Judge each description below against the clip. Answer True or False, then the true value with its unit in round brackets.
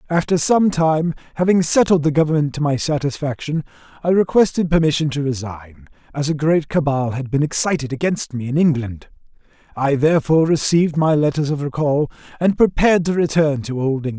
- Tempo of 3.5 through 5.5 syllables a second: False (5.7 syllables/s)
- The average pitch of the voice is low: False (150 Hz)